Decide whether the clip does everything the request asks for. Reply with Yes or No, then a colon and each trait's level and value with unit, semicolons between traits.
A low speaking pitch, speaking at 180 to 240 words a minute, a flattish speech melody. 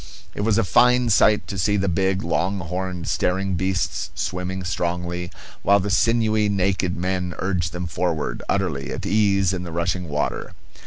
No: very low, 95 Hz; average, 165 wpm; narrow, 2.1 semitones